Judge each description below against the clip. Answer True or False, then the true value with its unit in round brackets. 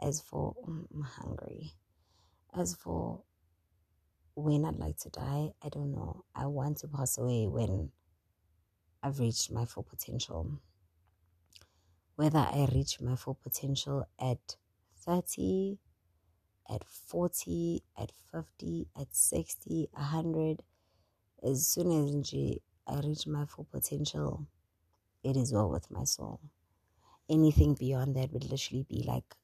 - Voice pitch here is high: False (105 Hz)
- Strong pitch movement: True (8.4 semitones)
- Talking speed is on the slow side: True (125 wpm)